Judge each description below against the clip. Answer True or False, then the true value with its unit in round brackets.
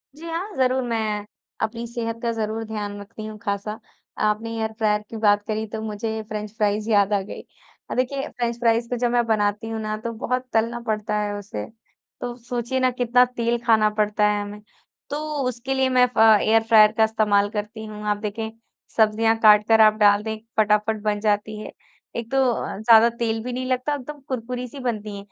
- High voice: True (220 Hz)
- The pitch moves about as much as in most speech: False (2.1 semitones)